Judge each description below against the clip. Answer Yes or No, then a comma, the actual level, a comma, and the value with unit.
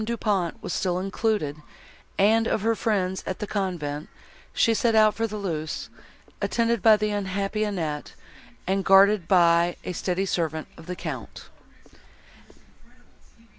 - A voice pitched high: Yes, high, 195 Hz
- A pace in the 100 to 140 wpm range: Yes, slow, 135 wpm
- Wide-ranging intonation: No, average, 3.6 semitones